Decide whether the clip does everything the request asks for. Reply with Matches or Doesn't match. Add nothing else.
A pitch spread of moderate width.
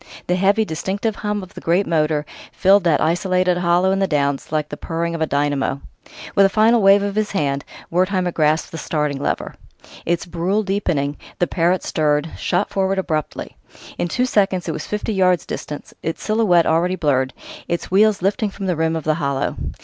Matches